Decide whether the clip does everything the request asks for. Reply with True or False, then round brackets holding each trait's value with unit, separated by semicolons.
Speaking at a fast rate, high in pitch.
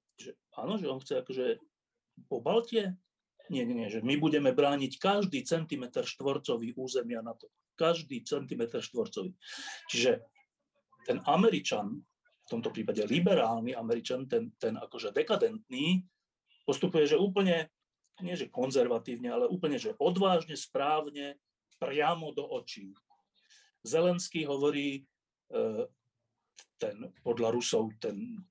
False (115 wpm; 195 Hz)